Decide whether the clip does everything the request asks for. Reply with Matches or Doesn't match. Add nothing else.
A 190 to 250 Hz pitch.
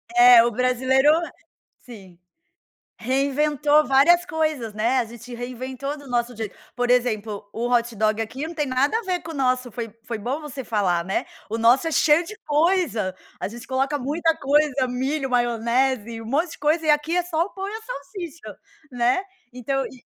Doesn't match